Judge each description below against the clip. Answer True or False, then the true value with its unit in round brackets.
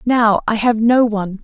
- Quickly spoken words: True (210 wpm)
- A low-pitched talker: False (225 Hz)